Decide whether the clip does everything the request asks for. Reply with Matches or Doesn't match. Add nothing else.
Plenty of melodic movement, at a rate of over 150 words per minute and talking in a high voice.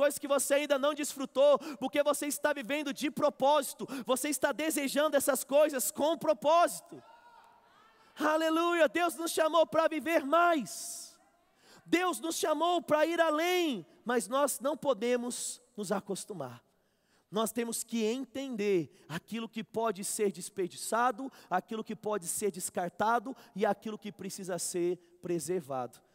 Doesn't match